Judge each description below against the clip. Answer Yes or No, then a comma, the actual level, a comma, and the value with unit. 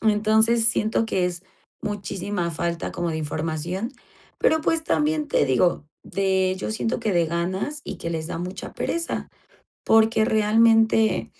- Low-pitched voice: No, high, 205 Hz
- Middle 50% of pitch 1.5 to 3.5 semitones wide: No, average, 4.5 semitones